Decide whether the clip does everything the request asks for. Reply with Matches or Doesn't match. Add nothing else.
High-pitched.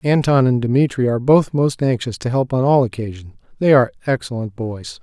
Doesn't match